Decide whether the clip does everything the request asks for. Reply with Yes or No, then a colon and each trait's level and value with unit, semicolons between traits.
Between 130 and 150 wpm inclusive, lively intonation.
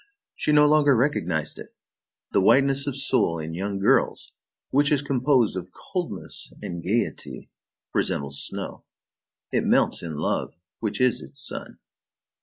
Yes: average, 140 wpm; wide, 8.3 semitones